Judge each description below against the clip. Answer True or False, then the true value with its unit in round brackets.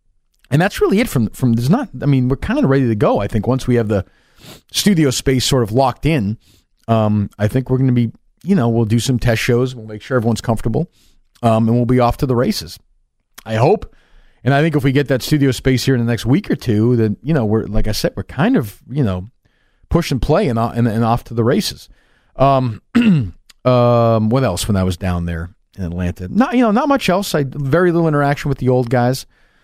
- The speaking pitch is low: True (125 Hz)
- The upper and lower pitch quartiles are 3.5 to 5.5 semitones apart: True (4.1 semitones)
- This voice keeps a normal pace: False (245 wpm)